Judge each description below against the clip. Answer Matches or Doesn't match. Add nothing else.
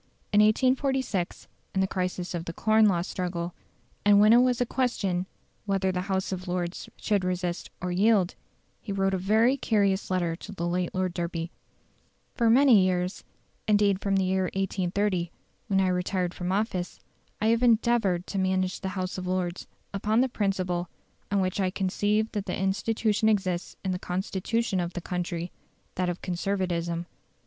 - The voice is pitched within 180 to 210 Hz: Matches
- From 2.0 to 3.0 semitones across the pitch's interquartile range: Matches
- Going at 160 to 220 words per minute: Matches